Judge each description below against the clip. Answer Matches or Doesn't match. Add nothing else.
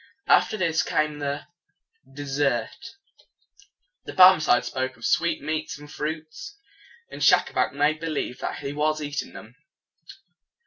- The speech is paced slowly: Matches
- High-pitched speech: Doesn't match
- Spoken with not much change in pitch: Matches